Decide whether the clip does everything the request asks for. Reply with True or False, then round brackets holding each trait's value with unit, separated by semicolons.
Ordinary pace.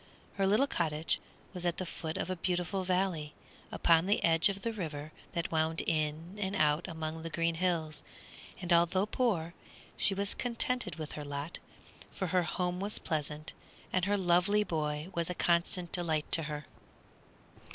True (170 wpm)